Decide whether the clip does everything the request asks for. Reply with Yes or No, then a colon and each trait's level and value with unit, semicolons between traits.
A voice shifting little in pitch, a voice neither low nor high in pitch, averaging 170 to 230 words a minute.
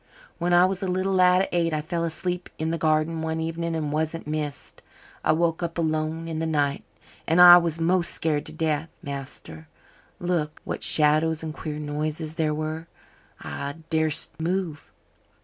Yes: narrow, 1.7 semitones; medium, 160 Hz; average, 175 wpm